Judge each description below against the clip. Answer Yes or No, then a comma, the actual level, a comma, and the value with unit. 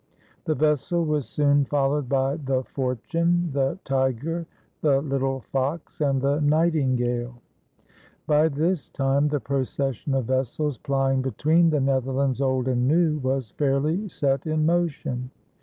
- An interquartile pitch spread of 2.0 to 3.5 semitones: Yes, narrow, 2.6 semitones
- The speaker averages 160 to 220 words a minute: No, slow, 135 wpm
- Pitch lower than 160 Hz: Yes, medium, 140 Hz